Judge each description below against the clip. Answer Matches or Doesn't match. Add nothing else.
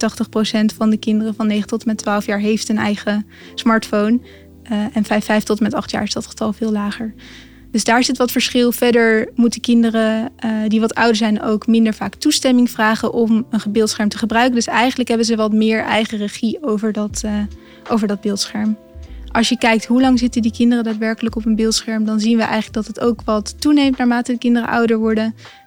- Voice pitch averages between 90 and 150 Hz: Doesn't match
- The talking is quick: Matches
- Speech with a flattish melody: Matches